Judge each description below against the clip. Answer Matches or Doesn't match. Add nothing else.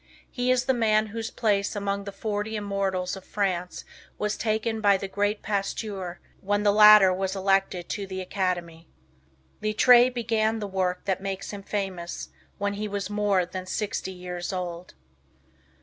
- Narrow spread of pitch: Matches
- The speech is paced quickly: Doesn't match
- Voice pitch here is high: Matches